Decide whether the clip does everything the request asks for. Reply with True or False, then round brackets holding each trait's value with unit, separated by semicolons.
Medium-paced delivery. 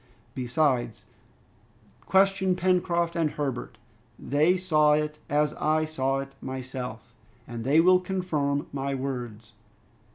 False (110 wpm)